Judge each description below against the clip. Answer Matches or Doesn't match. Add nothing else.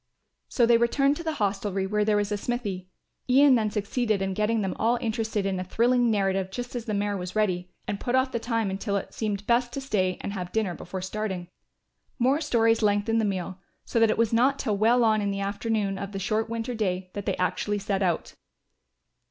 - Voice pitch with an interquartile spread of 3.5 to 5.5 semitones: Doesn't match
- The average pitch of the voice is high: Matches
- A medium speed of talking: Doesn't match